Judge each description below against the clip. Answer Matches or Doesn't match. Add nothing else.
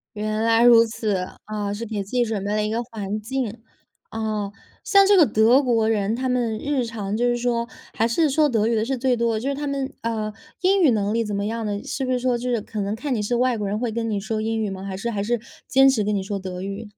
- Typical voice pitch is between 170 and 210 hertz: Doesn't match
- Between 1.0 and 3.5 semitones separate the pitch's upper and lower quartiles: Matches